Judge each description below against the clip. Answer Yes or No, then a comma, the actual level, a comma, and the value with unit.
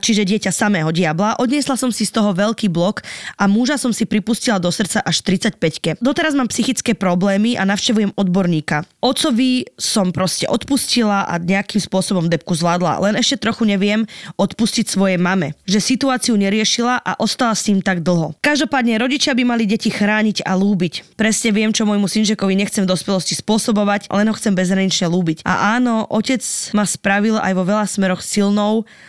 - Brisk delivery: Yes, fast, 175 wpm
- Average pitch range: Yes, average, 3.1 semitones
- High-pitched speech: Yes, high, 210 Hz